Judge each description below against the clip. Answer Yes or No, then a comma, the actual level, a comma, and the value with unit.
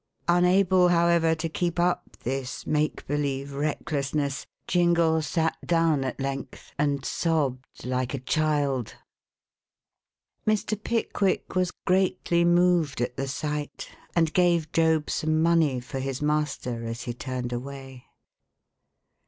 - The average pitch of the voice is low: No, medium, 150 Hz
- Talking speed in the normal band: No, slow, 120 wpm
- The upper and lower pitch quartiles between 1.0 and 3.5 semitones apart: No, average, 4.2 semitones